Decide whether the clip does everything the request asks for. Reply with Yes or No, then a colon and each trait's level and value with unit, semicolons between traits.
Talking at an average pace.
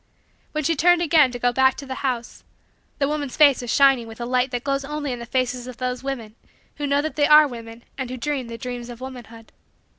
No: fast, 240 wpm